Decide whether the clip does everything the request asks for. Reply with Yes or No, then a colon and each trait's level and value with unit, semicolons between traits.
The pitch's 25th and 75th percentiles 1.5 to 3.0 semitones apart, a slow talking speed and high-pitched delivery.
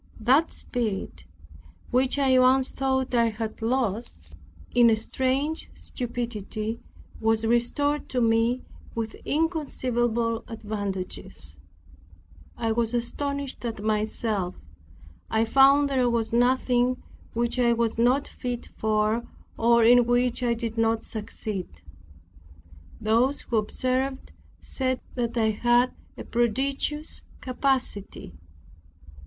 Yes: narrow, 2.5 semitones; slow, 110 wpm; high, 235 Hz